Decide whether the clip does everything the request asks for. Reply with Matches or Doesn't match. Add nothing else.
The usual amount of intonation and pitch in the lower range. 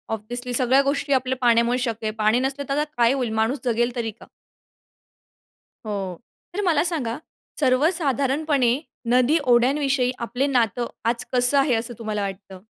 Doesn't match